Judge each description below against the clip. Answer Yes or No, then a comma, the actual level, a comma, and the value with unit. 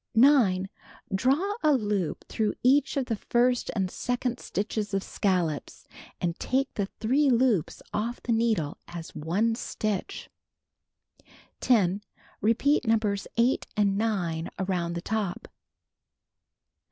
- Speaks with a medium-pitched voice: No, high, 215 Hz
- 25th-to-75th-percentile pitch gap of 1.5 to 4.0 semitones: No, average, 4.5 semitones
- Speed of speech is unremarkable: No, slow, 120 wpm